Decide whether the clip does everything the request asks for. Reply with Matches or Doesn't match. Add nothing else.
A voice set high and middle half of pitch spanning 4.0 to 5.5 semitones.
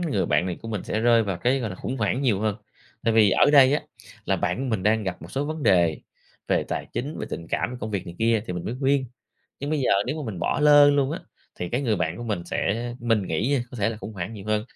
Doesn't match